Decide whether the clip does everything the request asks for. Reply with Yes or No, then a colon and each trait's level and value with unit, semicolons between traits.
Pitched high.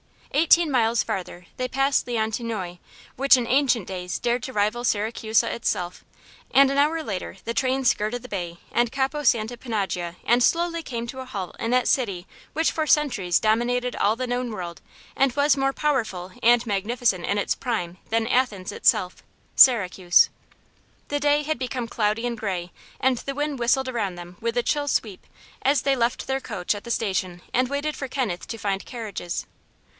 Yes: high, 235 Hz